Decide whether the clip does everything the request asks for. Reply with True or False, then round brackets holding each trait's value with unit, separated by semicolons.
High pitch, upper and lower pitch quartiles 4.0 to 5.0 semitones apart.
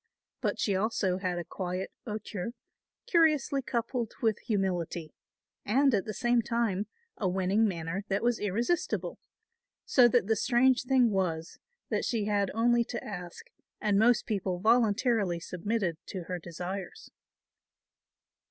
True (210 Hz; 4.3 semitones)